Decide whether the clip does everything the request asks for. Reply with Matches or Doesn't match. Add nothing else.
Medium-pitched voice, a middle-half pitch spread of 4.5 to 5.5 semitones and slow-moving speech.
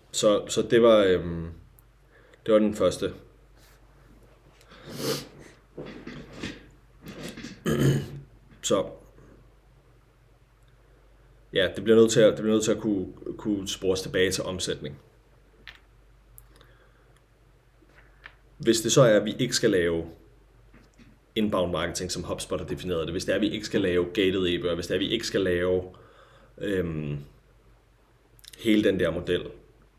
Doesn't match